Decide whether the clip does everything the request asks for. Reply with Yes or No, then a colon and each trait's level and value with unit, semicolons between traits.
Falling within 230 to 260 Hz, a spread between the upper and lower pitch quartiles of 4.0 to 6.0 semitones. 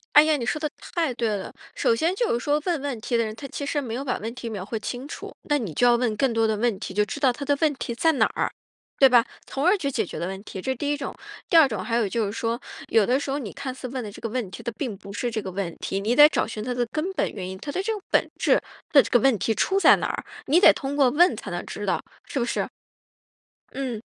Yes: high, 245 Hz; average, 4.5 semitones